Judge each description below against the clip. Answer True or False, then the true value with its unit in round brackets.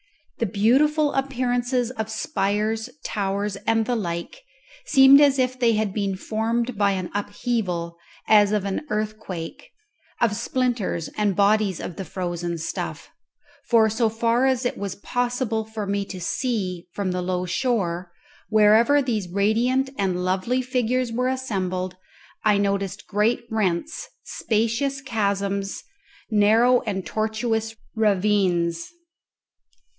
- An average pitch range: True (3.8 semitones)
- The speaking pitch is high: True (215 Hz)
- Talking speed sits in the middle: False (130 wpm)